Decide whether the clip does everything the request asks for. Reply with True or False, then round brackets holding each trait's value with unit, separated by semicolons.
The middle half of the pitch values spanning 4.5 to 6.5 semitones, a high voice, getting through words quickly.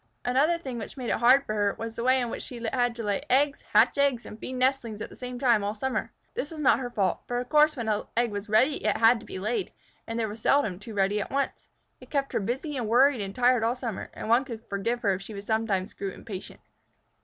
False (3.4 semitones; 235 Hz; 260 wpm)